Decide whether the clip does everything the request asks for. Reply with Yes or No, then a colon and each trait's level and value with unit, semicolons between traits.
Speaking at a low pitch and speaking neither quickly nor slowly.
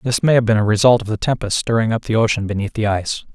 No: low, 110 Hz; fast, 285 wpm